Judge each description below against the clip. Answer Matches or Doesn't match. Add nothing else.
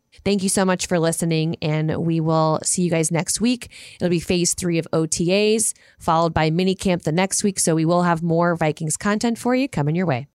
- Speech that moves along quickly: Matches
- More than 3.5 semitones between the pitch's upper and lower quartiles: Doesn't match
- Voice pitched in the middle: Matches